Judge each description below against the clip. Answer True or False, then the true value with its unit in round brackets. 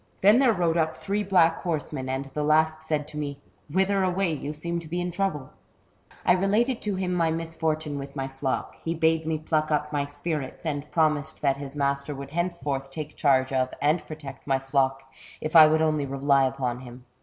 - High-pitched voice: False (155 Hz)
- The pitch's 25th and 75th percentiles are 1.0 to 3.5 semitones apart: True (3.2 semitones)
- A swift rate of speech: True (210 wpm)